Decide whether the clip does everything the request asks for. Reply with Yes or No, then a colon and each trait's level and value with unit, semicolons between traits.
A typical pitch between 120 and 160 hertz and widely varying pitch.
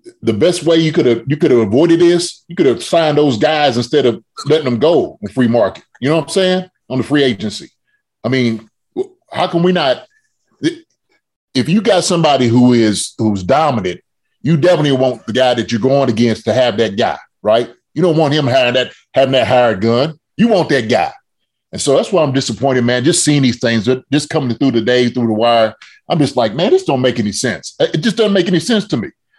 Yes: low, 135 Hz; wide, 6.0 semitones